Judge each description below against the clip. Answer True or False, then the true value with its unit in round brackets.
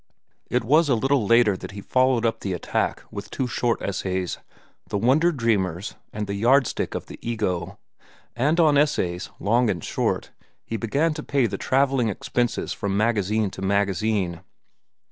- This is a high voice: False (115 Hz)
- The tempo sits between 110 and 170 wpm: True (165 wpm)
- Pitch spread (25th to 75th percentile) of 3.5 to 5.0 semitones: True (4.7 semitones)